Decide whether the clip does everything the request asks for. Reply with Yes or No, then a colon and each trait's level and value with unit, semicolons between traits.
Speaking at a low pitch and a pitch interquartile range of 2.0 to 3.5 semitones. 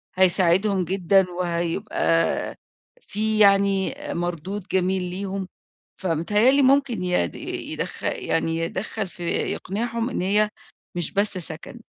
No: high, 190 Hz; average, 2.9 semitones